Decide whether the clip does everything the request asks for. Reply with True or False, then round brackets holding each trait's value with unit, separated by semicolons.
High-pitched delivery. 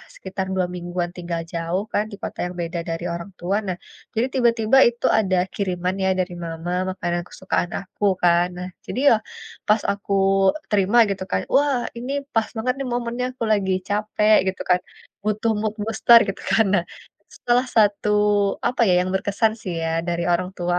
True (195 Hz)